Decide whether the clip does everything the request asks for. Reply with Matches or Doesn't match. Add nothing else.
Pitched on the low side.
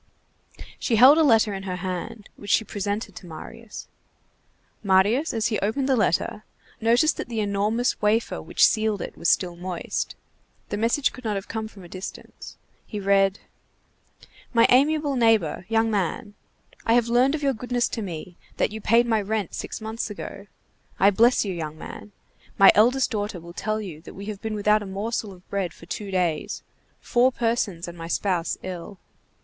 Doesn't match